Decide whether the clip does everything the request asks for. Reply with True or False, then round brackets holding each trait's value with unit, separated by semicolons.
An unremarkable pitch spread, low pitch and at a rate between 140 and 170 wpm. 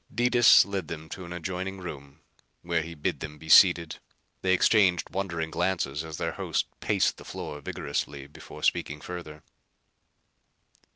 True (3.5 semitones; 85 Hz; 150 wpm)